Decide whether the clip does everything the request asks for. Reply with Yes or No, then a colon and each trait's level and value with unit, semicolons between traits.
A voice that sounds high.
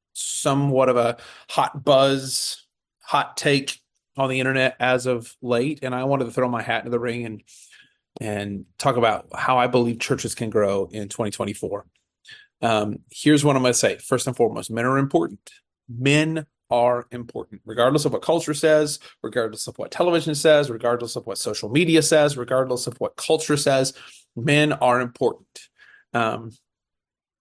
No: low, 125 Hz